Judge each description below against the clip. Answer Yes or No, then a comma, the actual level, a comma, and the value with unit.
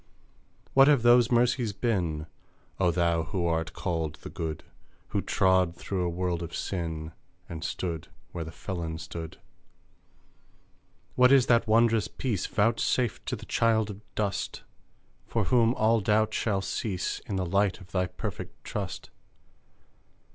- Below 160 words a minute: Yes, average, 145 wpm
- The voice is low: Yes, very low, 95 Hz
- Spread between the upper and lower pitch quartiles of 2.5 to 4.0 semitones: No, average, 5.1 semitones